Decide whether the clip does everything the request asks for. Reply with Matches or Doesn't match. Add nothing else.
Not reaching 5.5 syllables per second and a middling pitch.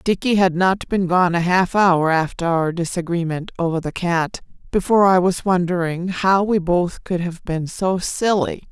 Matches